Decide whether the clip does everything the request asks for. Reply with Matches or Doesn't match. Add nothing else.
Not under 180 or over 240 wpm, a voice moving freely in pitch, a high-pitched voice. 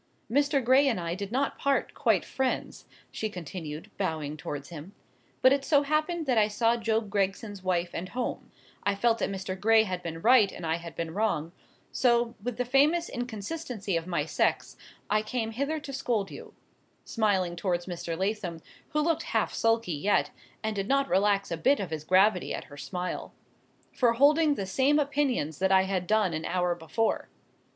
Matches